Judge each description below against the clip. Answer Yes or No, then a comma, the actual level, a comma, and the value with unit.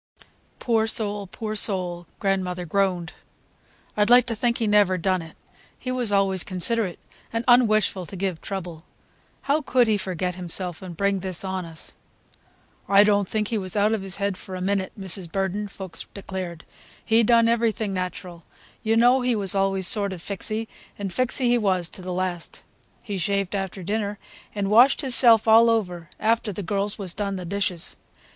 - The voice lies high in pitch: Yes, high, 200 Hz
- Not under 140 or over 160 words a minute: No, average, 180 wpm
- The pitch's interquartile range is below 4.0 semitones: Yes, average, 3.1 semitones